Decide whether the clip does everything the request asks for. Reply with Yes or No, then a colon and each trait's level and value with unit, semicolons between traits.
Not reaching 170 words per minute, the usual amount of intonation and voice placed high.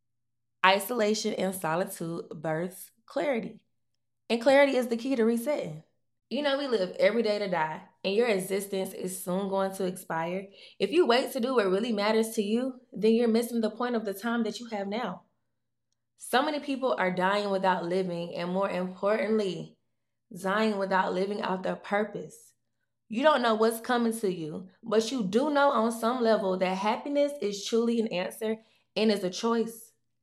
No: average, 180 wpm; average, 3.8 semitones; high, 210 Hz